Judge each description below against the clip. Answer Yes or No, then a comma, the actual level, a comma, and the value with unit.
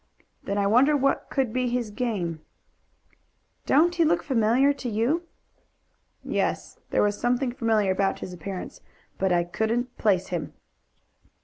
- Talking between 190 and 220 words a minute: No, average, 140 wpm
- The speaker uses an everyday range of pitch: Yes, average, 5.0 semitones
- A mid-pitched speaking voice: No, high, 230 Hz